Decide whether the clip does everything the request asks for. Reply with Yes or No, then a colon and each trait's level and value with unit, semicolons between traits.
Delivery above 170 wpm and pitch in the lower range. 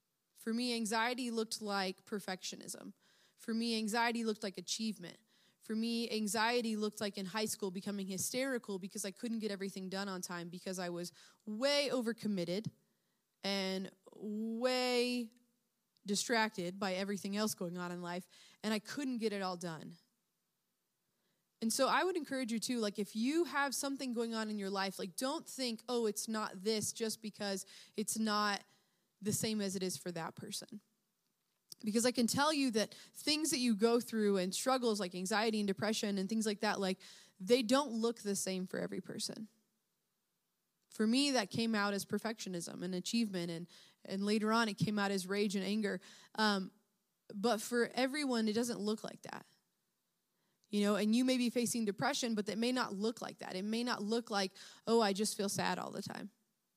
No: average, 185 wpm; high, 210 Hz